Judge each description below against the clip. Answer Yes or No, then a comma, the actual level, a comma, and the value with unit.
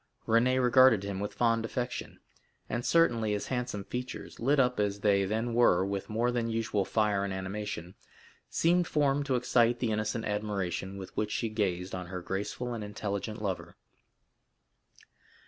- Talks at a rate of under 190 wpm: Yes, average, 160 wpm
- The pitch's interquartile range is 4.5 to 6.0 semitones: No, average, 3.5 semitones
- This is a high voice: No, low, 110 Hz